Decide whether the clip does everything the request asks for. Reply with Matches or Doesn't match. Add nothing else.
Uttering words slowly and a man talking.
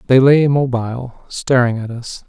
Matches